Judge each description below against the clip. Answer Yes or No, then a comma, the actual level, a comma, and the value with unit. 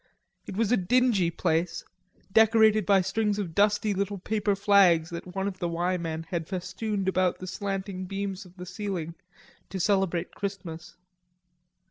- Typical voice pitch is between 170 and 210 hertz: Yes, high, 190 Hz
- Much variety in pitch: No, narrow, 2.5 semitones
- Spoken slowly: No, average, 155 wpm